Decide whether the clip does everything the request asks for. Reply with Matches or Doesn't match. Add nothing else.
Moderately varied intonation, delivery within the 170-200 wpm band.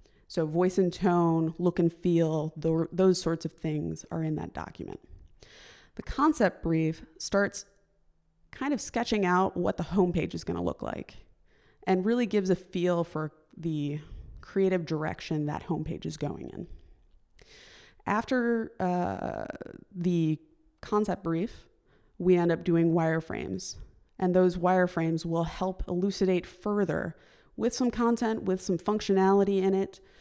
Doesn't match